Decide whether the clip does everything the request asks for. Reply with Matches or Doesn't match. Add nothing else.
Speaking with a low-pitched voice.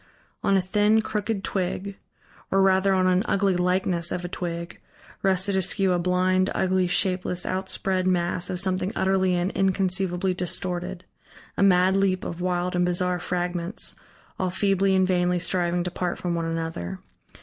Doesn't match